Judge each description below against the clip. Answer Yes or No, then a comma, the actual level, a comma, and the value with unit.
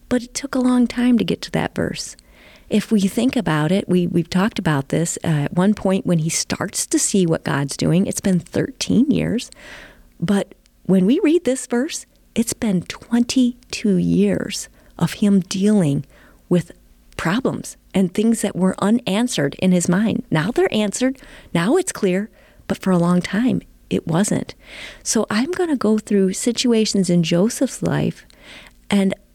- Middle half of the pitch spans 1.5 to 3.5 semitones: No, average, 5.1 semitones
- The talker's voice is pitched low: No, high, 205 Hz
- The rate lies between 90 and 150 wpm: No, average, 170 wpm